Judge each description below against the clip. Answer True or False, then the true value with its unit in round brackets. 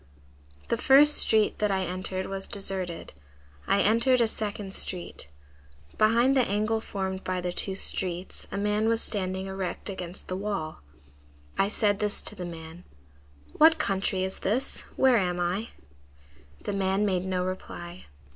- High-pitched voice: True (195 Hz)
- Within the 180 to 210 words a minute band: False (155 wpm)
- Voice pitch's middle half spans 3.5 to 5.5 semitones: False (2.5 semitones)